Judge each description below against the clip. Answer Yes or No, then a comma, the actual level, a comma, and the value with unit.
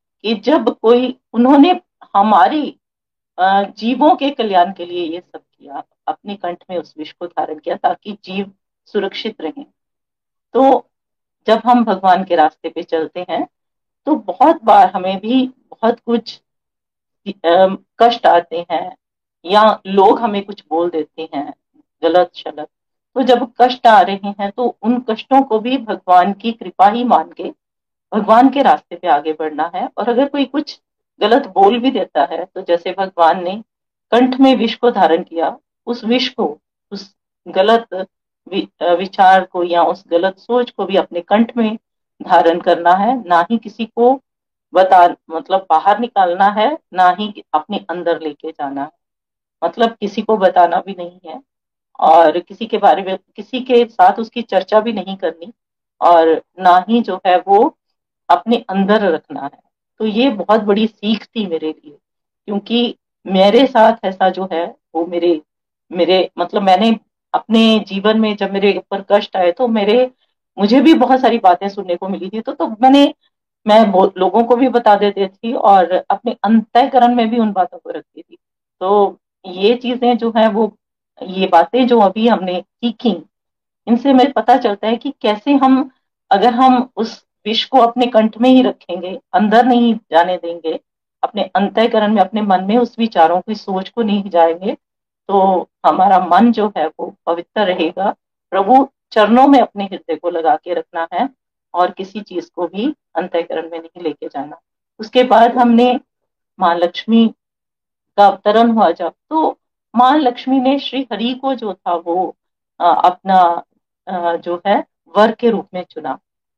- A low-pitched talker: No, high, 205 Hz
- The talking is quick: No, average, 165 wpm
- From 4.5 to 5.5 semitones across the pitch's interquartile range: Yes, average, 5.2 semitones